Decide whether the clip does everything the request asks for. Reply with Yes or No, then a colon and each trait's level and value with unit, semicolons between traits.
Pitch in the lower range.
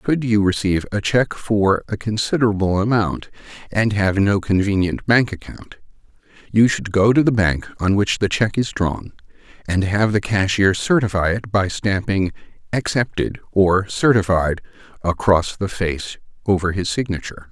Yes: low, 100 Hz